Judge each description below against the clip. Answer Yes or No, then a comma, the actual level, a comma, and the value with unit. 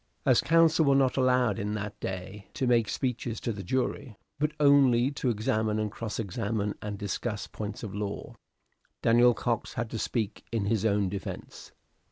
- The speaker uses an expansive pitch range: No, average, 3.4 semitones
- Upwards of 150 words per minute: Yes, average, 175 wpm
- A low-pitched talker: Yes, low, 115 Hz